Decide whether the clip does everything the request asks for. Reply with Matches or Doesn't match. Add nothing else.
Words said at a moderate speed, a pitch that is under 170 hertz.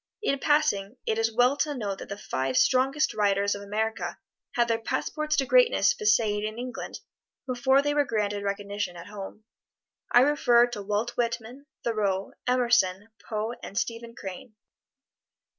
Doesn't match